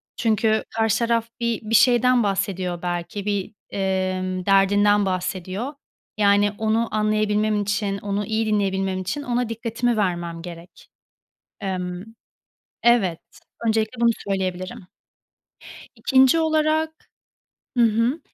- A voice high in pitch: Yes, high, 210 Hz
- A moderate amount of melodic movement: Yes, average, 3.3 semitones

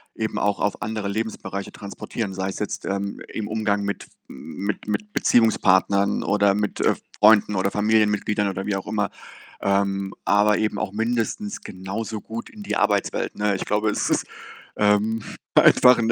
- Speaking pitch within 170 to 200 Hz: No, low, 105 Hz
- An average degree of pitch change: No, narrow, 1.8 semitones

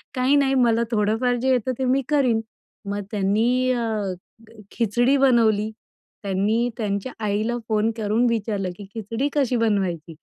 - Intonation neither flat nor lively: Yes, average, 3.4 semitones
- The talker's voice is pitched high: Yes, high, 230 Hz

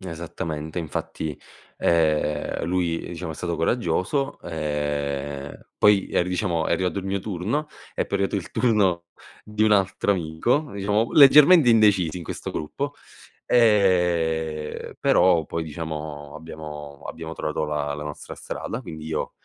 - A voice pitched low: Yes, very low, 85 Hz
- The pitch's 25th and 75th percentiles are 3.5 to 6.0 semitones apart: Yes, average, 4.6 semitones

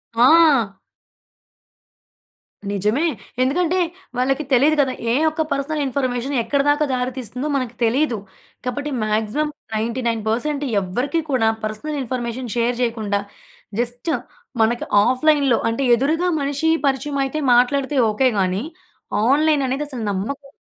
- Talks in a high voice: Yes, very high, 260 Hz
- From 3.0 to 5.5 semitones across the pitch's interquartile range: Yes, average, 3.6 semitones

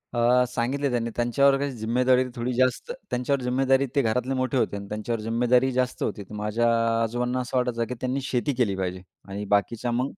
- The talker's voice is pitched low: Yes, low, 125 Hz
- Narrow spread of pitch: Yes, narrow, 1.9 semitones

